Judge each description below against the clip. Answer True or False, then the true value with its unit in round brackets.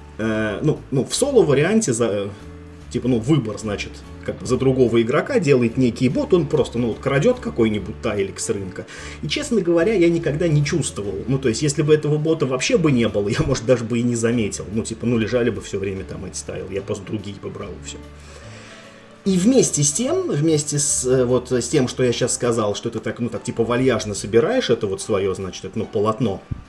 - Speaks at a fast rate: True (210 wpm)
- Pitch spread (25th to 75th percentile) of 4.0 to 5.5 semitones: True (5.1 semitones)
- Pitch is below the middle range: True (120 Hz)